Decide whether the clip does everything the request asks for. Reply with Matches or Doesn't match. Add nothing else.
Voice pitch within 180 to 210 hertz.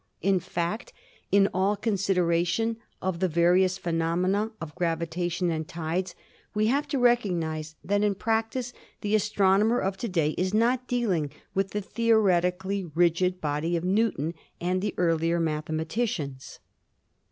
Matches